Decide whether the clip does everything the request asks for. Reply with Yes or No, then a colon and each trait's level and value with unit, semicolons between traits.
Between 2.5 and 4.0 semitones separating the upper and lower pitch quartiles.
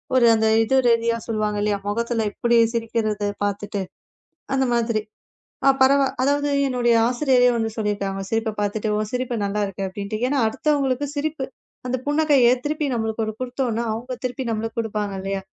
Yes: average, 3.3 semitones